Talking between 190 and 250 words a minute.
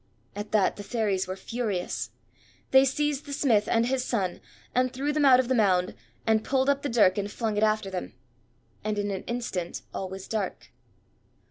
Yes: average, 195 wpm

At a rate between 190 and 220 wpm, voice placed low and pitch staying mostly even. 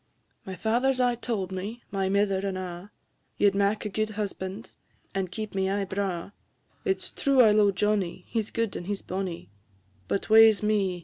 No: average, 200 wpm; high, 200 Hz; narrow, 2.3 semitones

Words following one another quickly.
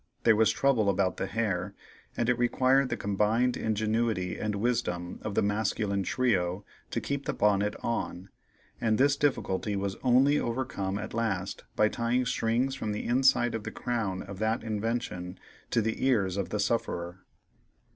No: average, 165 wpm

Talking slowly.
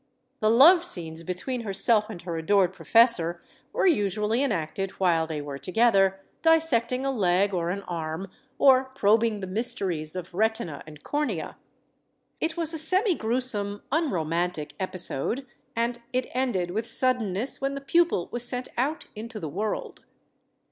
No: average, 145 wpm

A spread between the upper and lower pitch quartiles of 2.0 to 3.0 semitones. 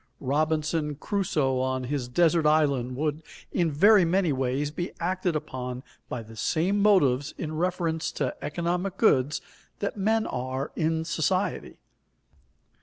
No: average, 4.9 semitones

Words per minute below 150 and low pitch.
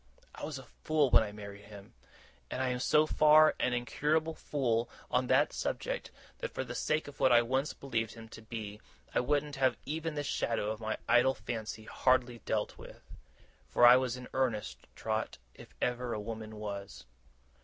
No: average, 185 wpm; low, 125 Hz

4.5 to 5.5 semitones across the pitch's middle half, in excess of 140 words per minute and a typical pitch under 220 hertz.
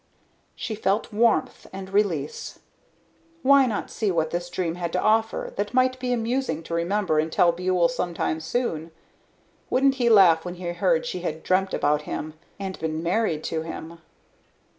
Yes: average, 5.1 semitones; average, 165 wpm; medium, 185 Hz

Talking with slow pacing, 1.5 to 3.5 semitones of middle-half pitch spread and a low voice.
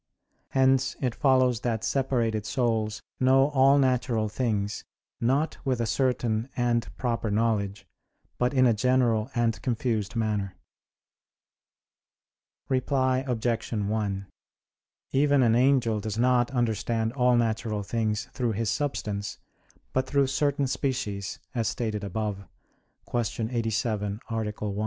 Yes: slow, 120 wpm; average, 3.1 semitones; low, 115 Hz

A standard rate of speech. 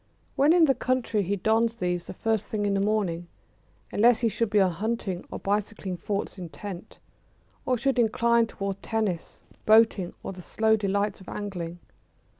Yes: average, 170 wpm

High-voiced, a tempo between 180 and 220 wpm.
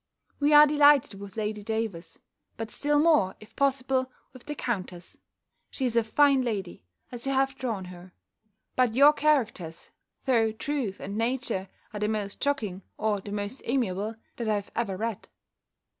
No: high, 225 Hz; average, 160 wpm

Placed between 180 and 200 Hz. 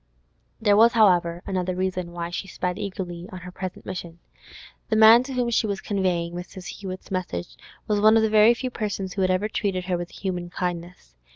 Yes: medium, 185 Hz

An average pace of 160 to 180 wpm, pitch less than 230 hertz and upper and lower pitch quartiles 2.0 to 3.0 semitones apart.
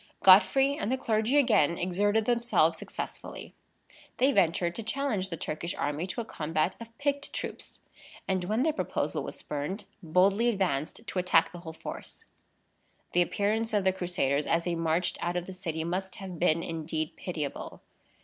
No: average, 170 wpm; medium, 185 Hz; average, 4.9 semitones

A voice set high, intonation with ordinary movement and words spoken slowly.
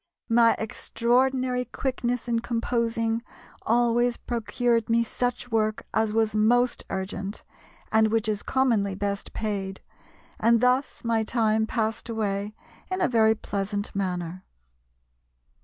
No: high, 225 Hz; narrow, 2.2 semitones; slow, 120 wpm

